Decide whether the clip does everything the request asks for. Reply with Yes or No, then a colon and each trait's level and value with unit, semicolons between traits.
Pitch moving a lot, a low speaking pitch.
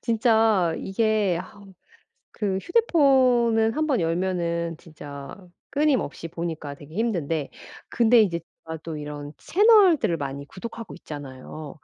No: wide, 6.8 semitones; medium, 185 Hz